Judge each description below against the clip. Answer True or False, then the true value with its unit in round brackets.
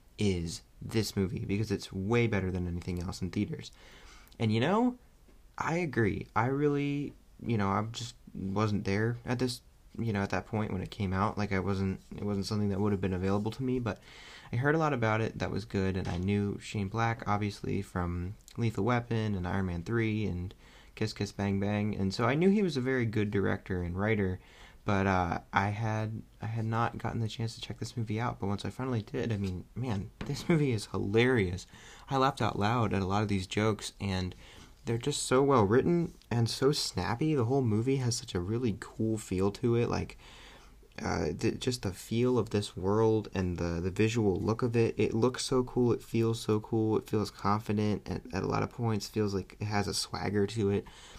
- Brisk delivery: True (220 wpm)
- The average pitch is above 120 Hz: False (105 Hz)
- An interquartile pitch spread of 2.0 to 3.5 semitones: True (3.2 semitones)